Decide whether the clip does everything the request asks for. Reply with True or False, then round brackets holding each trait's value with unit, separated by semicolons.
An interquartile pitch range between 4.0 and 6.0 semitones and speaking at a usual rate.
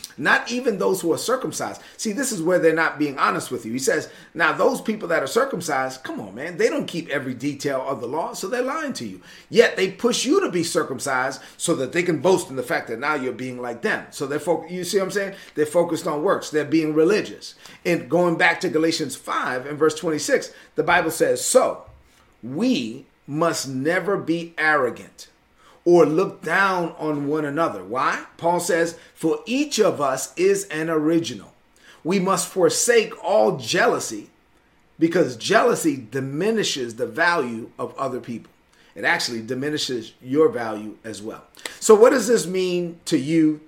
True (4.5 semitones; 190 wpm)